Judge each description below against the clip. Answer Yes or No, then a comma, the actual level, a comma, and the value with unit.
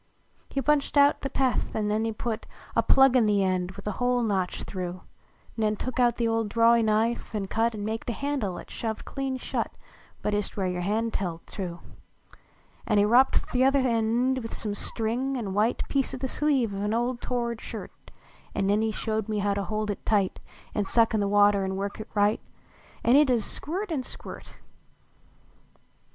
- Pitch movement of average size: Yes, average, 3.4 semitones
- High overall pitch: Yes, high, 220 Hz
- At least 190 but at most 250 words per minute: Yes, average, 200 wpm